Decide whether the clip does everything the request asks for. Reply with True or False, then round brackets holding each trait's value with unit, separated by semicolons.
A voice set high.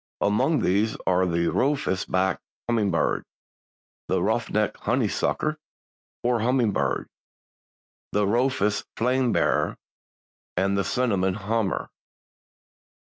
False (105 Hz)